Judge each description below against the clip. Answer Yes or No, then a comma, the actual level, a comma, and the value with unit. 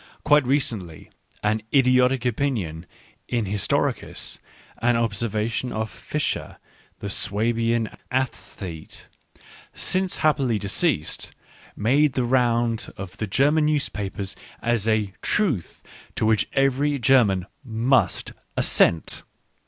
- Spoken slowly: Yes, slow, 105 wpm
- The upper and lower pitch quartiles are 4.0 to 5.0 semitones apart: Yes, average, 4.4 semitones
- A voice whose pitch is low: Yes, low, 115 Hz